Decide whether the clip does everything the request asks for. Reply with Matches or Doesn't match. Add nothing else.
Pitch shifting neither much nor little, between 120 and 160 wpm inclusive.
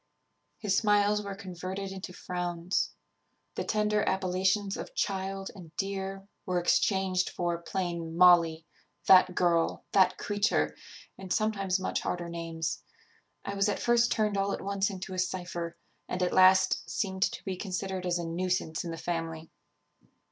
Doesn't match